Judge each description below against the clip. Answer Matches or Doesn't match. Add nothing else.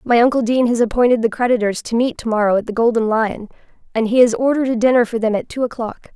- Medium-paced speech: Doesn't match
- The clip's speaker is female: Matches